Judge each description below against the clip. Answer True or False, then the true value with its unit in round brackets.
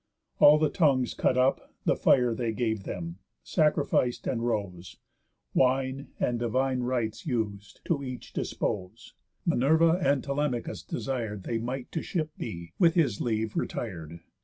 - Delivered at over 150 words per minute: False (140 wpm)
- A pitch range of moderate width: True (4.1 semitones)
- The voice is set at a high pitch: False (125 Hz)